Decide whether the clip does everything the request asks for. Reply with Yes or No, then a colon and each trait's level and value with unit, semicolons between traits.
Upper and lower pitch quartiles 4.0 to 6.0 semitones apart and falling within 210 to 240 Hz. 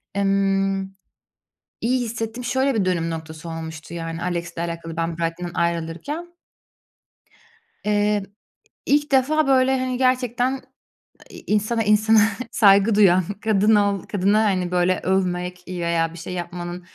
No: average, 4.7 semitones; high, 195 Hz